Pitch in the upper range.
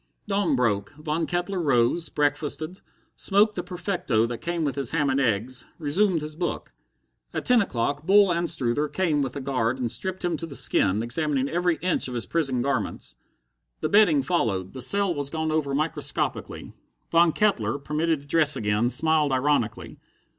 No: medium, 150 Hz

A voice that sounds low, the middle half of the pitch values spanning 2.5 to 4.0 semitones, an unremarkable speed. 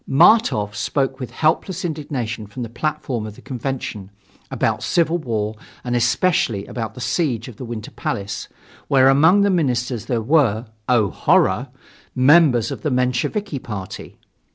No: low, 125 Hz; average, 5.2 semitones; average, 150 wpm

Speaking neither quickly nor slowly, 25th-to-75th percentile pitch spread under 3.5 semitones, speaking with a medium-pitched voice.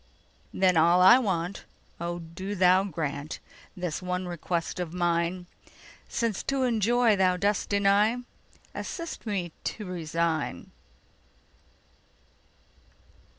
No: slow, 85 wpm; average, 3.1 semitones; medium, 180 Hz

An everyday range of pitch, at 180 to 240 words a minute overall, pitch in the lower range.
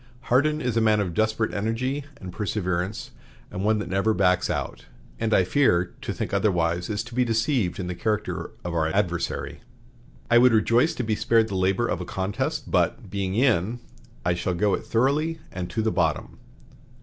Yes: average, 4.2 semitones; average, 190 wpm; low, 105 Hz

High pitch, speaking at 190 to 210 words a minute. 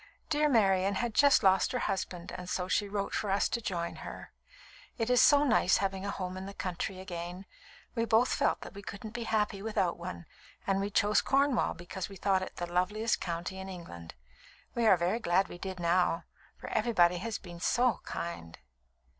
Yes: high, 195 Hz; average, 195 wpm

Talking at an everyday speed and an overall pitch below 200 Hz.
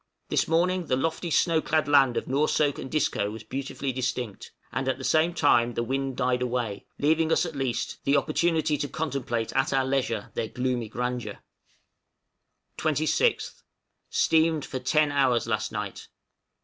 Yes: average, 170 wpm; low, 135 Hz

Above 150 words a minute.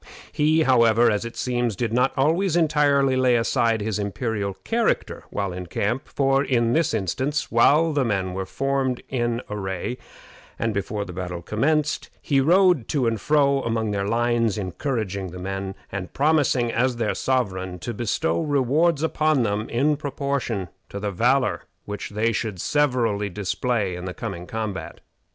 Yes: average, 160 wpm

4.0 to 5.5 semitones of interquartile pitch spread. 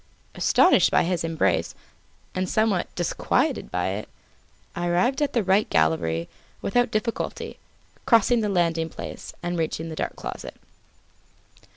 Yes: average, 5.0 semitones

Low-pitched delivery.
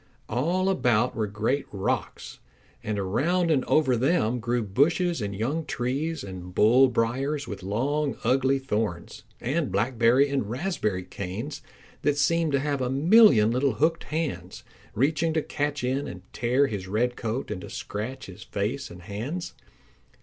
Yes: low, 125 Hz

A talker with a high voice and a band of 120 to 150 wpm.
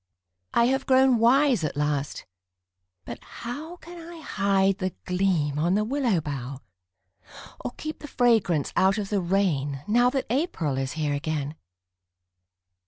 Yes: high, 195 Hz; average, 145 wpm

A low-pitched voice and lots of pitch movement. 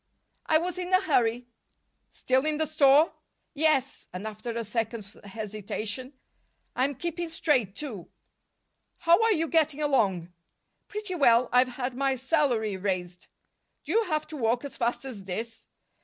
No: very high, 255 Hz; wide, 5.9 semitones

